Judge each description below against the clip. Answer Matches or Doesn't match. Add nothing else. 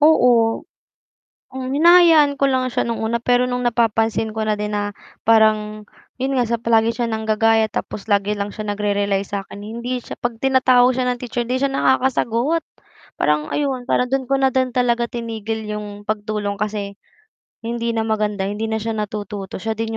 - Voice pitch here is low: Doesn't match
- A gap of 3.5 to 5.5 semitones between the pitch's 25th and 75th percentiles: Doesn't match